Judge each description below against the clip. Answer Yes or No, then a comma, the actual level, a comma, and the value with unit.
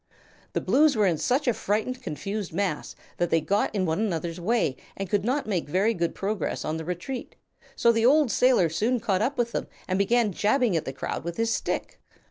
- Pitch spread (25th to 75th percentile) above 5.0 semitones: Yes, wide, 5.5 semitones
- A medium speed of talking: No, fast, 215 wpm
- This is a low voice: No, high, 205 Hz